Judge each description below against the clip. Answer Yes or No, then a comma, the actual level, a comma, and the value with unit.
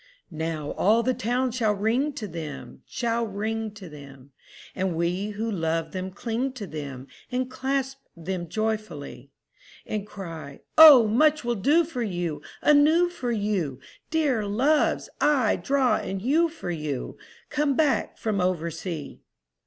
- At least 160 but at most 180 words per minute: No, average, 145 wpm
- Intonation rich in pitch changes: Yes, wide, 7.2 semitones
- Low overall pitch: No, high, 215 Hz